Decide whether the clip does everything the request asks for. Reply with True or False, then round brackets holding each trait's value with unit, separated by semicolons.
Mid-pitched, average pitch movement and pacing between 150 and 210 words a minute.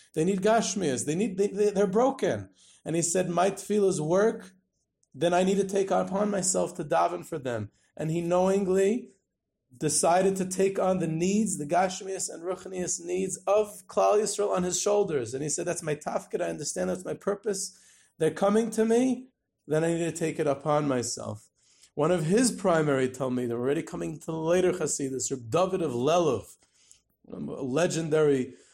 True (180 Hz; 4.6 semitones; 185 wpm)